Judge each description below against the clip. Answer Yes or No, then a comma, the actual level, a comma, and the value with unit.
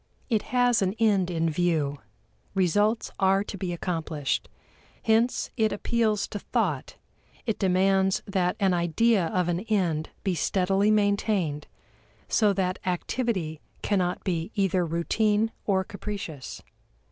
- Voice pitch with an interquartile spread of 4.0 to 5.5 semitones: No, average, 3.2 semitones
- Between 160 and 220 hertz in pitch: Yes, high, 190 Hz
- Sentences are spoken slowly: Yes, slow, 125 wpm